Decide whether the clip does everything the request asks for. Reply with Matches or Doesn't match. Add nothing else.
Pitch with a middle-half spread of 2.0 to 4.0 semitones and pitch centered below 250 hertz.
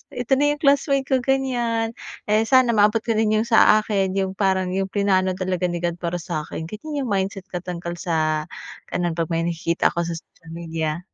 Doesn't match